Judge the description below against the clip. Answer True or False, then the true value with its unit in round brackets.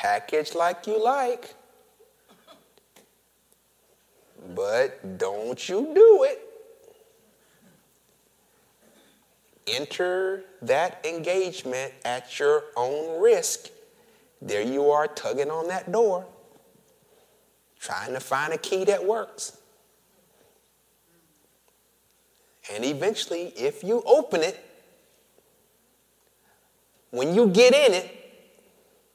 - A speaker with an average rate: False (85 wpm)